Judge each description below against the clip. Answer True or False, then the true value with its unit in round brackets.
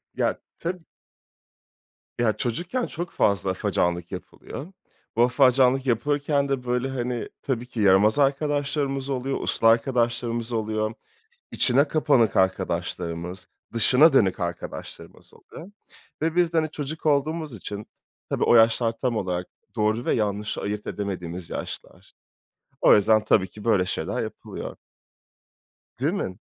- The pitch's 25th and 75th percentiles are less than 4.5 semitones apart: False (5.2 semitones)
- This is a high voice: False (120 Hz)